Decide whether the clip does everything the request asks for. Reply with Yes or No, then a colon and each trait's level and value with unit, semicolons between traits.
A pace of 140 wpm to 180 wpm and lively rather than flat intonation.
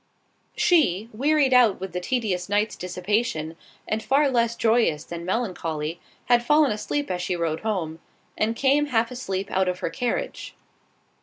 Yes: average, 155 wpm; wide, 5.7 semitones